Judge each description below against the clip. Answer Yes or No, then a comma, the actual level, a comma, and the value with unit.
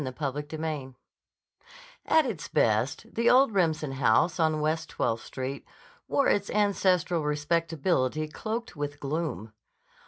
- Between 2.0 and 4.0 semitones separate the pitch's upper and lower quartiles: No, average, 4.6 semitones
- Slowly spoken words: Yes, slow, 120 wpm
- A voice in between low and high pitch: Yes, medium, 155 Hz